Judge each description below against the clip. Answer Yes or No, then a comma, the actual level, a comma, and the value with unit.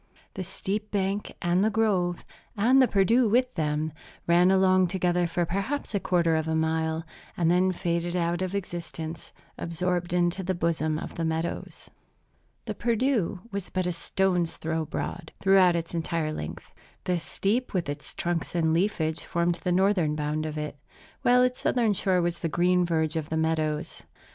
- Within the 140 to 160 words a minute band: No, average, 175 wpm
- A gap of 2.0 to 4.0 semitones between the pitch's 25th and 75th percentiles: Yes, average, 2.9 semitones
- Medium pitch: Yes, medium, 175 Hz